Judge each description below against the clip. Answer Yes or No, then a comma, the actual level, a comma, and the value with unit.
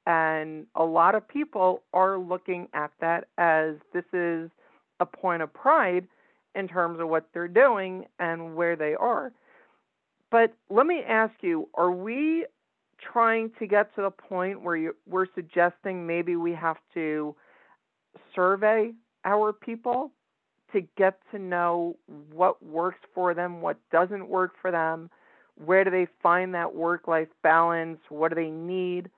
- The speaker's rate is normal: Yes, average, 155 wpm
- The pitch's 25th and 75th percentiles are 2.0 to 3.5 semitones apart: Yes, average, 2.9 semitones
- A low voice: No, medium, 180 Hz